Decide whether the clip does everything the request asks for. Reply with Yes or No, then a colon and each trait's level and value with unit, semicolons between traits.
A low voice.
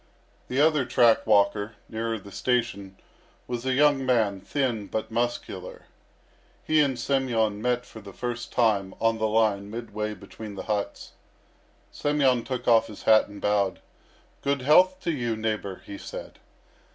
Yes: low, 115 Hz